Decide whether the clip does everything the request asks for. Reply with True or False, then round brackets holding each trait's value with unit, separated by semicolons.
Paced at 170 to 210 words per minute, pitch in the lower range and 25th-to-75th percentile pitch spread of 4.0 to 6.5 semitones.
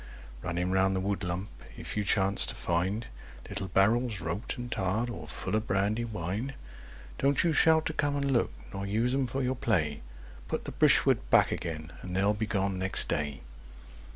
True (180 wpm; 100 Hz; 4.5 semitones)